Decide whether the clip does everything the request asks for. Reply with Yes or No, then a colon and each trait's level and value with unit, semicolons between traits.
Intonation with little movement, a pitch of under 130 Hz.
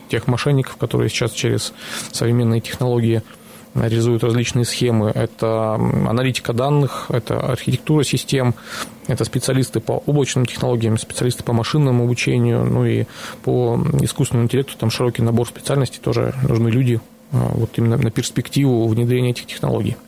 Yes: narrow, 2.1 semitones; low, 120 Hz